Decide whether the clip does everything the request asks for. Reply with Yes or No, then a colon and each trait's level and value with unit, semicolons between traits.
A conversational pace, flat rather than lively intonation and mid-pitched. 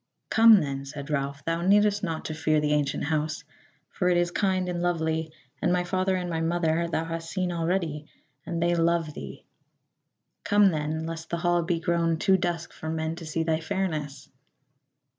Yes: average, 185 wpm; narrow, 1.9 semitones; medium, 165 Hz